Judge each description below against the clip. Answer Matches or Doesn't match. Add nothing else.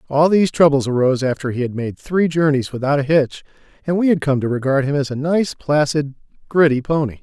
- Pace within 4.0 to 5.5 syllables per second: Doesn't match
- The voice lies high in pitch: Doesn't match